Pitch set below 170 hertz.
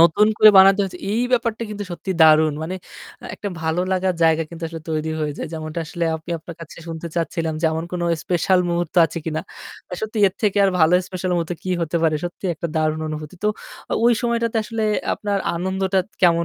No: medium, 175 Hz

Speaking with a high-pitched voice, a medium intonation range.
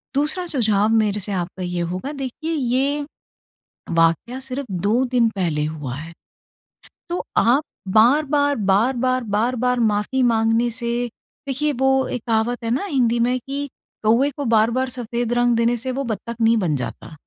Yes: high, 235 Hz; average, 3.6 semitones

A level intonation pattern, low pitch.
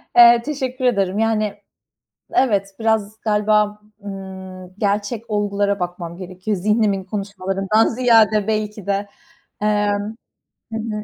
No: narrow, 1.9 semitones; high, 210 Hz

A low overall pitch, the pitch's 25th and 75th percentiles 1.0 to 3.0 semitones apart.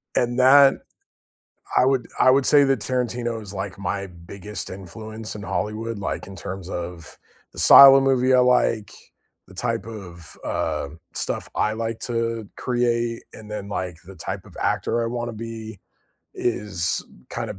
No: low, 110 Hz; average, 3.7 semitones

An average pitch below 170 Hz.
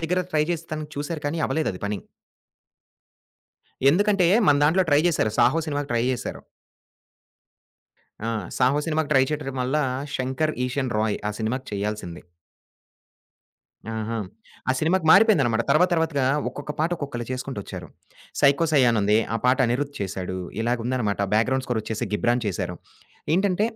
Yes: low, 135 Hz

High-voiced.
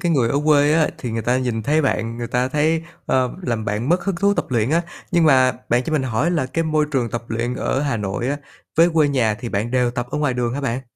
No: low, 130 Hz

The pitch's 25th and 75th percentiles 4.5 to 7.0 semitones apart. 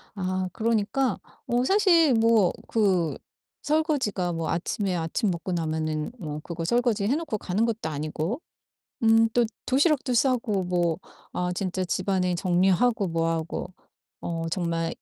Yes: wide, 5.4 semitones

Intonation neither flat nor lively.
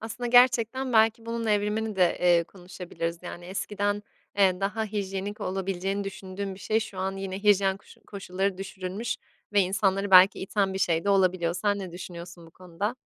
No: narrow, 2.1 semitones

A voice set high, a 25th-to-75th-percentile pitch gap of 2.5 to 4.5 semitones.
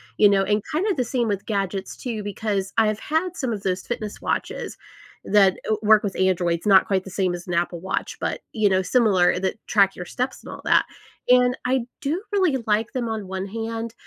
Yes: high, 210 Hz; average, 3.9 semitones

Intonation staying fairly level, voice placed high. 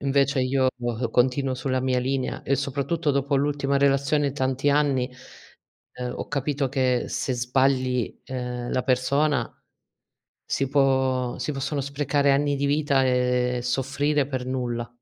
No: narrow, 1.8 semitones; low, 135 Hz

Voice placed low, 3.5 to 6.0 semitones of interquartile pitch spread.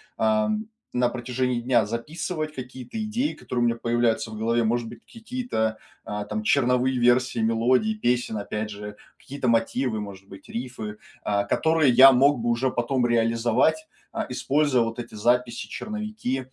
No: low, 120 Hz; average, 2.8 semitones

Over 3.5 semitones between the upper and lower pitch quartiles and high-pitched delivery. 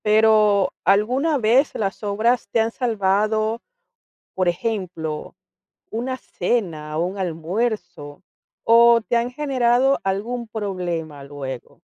Yes: average, 4.9 semitones; high, 215 Hz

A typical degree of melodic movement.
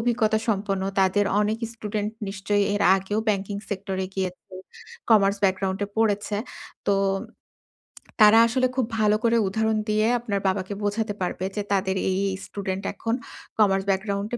No: narrow, 2.0 semitones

